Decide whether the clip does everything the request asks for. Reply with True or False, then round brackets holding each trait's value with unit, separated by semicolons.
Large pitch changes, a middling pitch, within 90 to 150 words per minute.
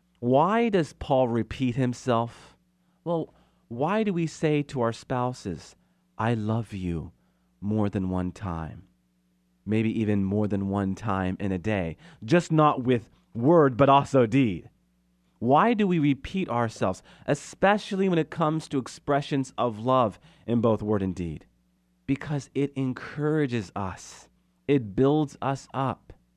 False (7.3 semitones; 120 Hz; 140 wpm)